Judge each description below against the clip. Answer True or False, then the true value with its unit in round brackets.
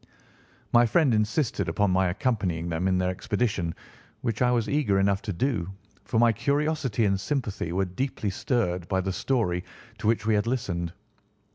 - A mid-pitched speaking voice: False (105 Hz)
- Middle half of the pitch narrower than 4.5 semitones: False (4.8 semitones)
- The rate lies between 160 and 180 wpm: True (170 wpm)